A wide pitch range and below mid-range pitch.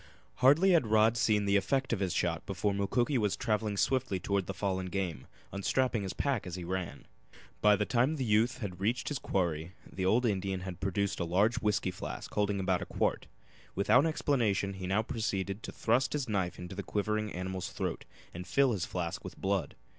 No: average, 3.8 semitones; low, 100 Hz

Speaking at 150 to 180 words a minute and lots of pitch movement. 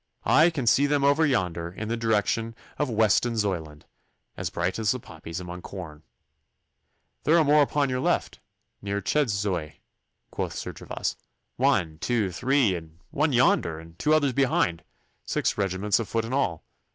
Yes: average, 160 wpm; wide, 7.2 semitones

